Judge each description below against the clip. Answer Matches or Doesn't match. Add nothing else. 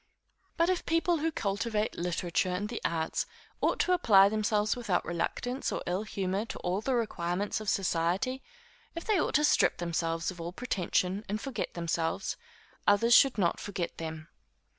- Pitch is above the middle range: Matches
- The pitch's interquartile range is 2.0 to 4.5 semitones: Doesn't match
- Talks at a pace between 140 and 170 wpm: Matches